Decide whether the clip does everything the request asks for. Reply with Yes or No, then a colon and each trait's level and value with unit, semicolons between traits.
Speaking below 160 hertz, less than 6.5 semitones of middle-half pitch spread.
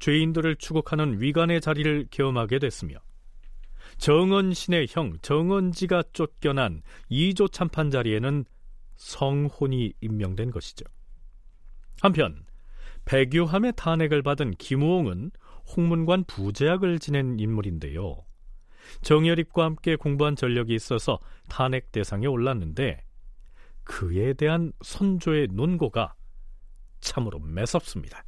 No: medium, 140 Hz; wide, 7.1 semitones